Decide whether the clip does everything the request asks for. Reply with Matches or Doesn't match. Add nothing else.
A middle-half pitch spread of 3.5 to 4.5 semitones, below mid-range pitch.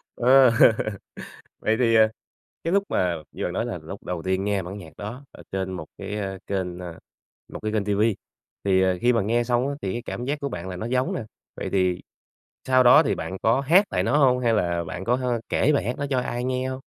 Doesn't match